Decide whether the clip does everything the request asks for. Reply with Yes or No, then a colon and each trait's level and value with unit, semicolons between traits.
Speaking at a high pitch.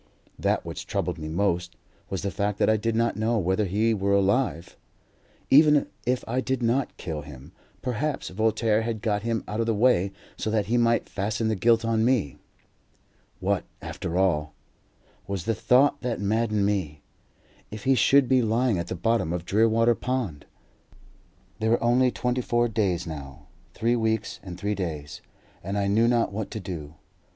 No: low, 110 Hz